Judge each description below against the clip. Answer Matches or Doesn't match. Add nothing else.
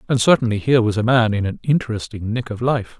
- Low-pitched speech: Matches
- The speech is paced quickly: Matches